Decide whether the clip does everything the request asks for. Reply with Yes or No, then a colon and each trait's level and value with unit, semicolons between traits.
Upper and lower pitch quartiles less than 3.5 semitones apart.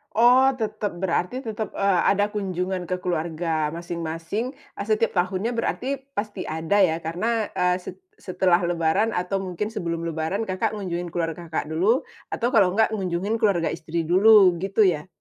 No: average, 3.9 semitones